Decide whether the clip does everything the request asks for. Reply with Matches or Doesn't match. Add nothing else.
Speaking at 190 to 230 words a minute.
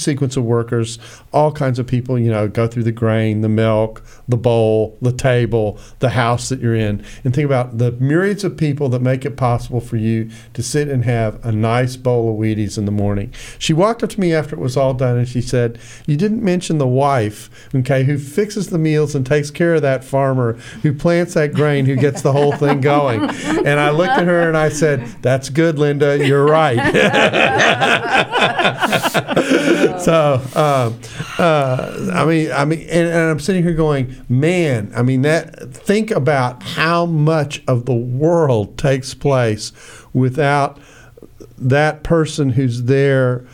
Doesn't match